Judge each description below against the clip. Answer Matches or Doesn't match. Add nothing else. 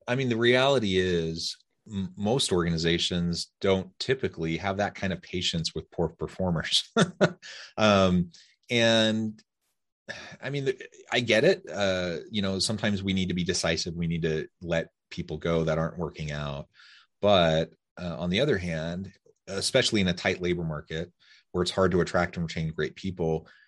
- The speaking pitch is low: Matches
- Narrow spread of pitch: Doesn't match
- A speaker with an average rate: Matches